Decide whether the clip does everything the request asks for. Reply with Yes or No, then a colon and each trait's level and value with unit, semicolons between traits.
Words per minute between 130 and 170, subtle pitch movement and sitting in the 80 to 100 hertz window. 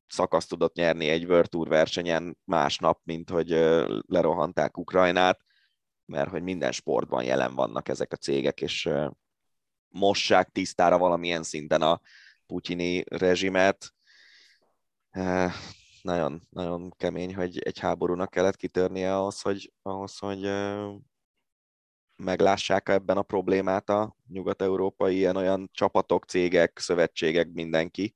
No: average, 110 wpm; narrow, 2.2 semitones; very low, 90 Hz